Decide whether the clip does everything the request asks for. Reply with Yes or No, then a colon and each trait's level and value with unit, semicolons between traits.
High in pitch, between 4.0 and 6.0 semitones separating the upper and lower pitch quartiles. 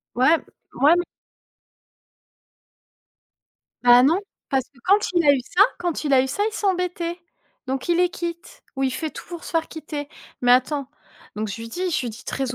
Yes: very high, 300 Hz; average, 5.0 semitones